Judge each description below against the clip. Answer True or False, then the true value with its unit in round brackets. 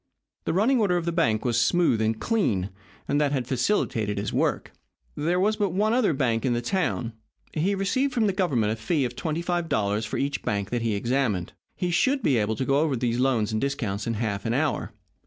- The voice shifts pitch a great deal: True (8.0 semitones)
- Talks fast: True (225 wpm)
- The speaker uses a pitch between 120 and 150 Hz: True (135 Hz)